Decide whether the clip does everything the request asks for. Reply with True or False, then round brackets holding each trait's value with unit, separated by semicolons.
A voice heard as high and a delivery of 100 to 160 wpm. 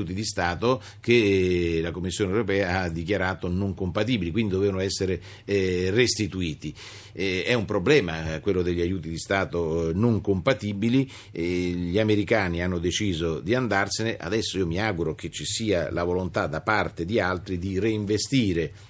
False (95 Hz; 145 wpm)